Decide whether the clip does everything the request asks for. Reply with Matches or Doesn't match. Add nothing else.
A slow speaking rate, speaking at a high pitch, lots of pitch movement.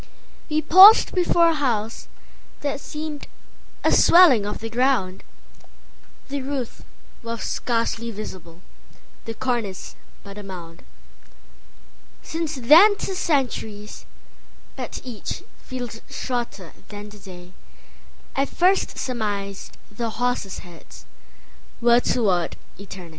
Matches